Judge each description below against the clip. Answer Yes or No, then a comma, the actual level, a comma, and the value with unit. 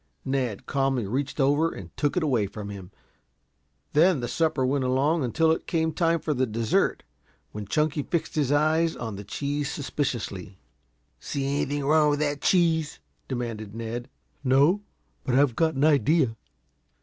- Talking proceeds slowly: No, average, 160 wpm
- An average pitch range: Yes, average, 4.3 semitones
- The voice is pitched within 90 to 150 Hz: Yes, medium, 140 Hz